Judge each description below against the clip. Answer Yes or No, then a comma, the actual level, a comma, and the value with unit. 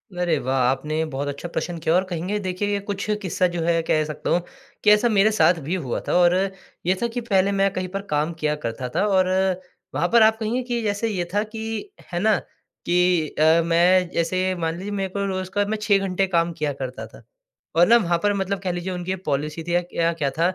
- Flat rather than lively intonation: No, average, 3.4 semitones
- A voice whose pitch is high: No, medium, 180 Hz